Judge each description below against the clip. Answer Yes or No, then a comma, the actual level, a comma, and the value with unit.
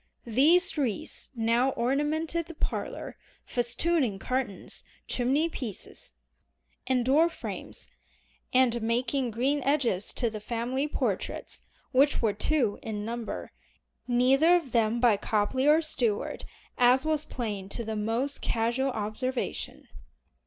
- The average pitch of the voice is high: Yes, very high, 250 Hz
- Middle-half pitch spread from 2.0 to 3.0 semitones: No, average, 3.8 semitones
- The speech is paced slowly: Yes, slow, 120 wpm